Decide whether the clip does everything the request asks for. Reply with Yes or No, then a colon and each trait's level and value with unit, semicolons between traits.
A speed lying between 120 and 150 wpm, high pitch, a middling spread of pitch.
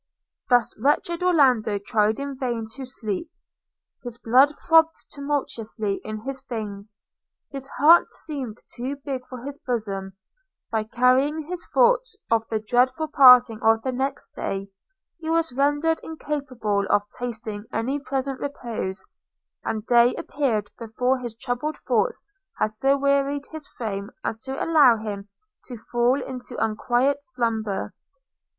Yes: average, 140 wpm; very high, 250 Hz; average, 4.1 semitones